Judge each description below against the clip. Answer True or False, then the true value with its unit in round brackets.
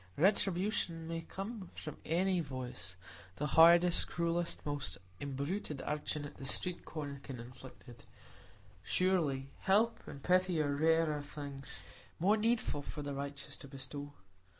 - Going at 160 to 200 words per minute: False (135 wpm)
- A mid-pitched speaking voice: True (150 Hz)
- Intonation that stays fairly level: False (4.2 semitones)